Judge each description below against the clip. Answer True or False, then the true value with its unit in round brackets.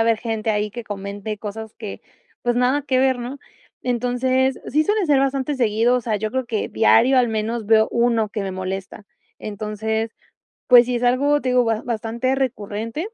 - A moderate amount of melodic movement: True (3.0 semitones)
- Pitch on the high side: True (235 Hz)